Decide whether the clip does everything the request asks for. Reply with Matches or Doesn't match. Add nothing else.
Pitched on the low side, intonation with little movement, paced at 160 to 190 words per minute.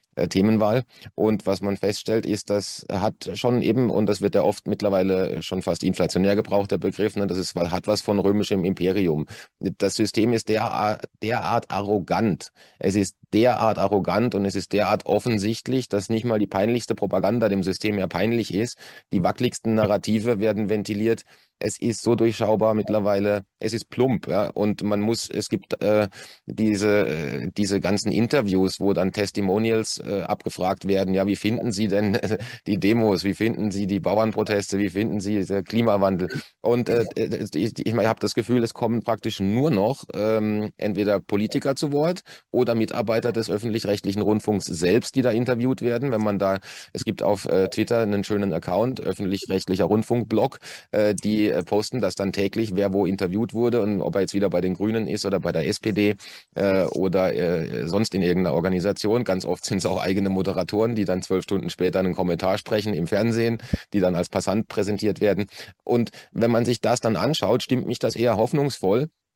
Matches